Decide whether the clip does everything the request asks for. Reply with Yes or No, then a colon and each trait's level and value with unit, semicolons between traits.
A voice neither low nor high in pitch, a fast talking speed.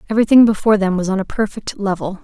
No: high, 205 Hz; fast, 215 wpm